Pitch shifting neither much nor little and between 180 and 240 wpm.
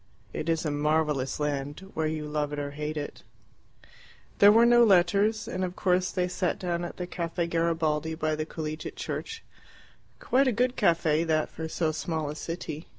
Yes: average, 3.0 semitones; average, 185 wpm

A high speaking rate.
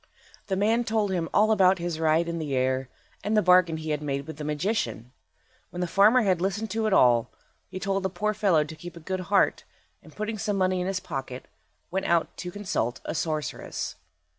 Yes: fast, 215 wpm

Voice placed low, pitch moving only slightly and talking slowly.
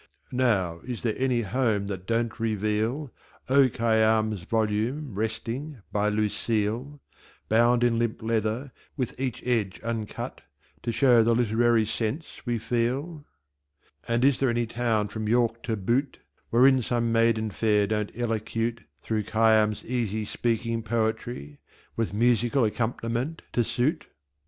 Yes: low, 115 Hz; narrow, 2.0 semitones; slow, 130 wpm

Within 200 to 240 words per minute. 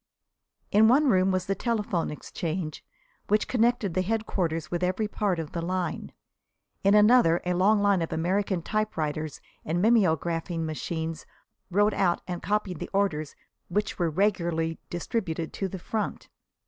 No: average, 150 wpm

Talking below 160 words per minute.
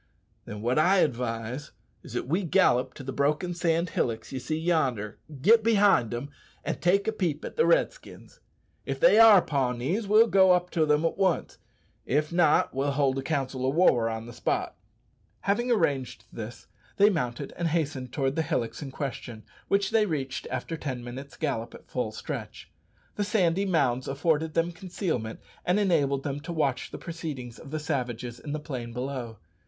No: average, 180 wpm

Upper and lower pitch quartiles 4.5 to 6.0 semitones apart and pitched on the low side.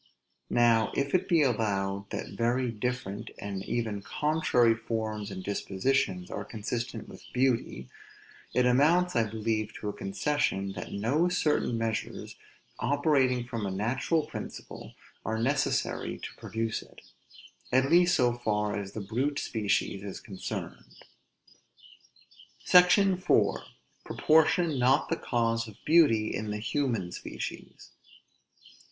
Yes: average, 4.9 semitones; low, 115 Hz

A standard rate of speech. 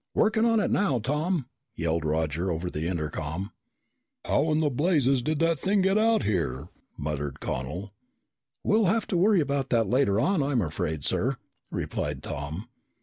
Yes: average, 150 wpm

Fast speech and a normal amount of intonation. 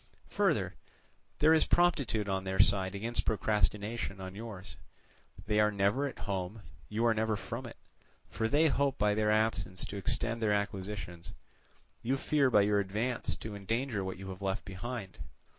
No: average, 165 wpm; average, 3.0 semitones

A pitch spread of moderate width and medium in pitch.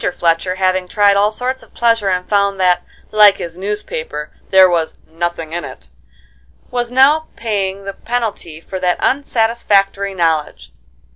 No: average, 3.7 semitones; high, 195 Hz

